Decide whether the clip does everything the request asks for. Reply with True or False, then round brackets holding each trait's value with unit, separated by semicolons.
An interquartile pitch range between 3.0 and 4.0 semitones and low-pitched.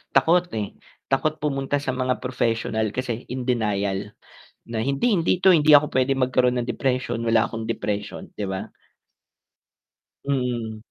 True (3.6 semitones; 125 Hz)